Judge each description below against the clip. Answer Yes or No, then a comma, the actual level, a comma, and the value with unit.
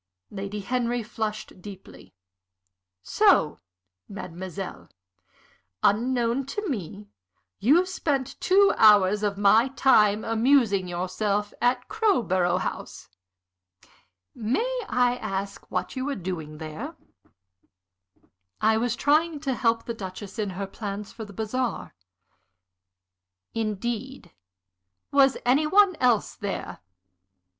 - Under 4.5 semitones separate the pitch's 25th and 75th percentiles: No, average, 4.9 semitones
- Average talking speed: No, slow, 105 wpm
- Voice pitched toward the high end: Yes, high, 220 Hz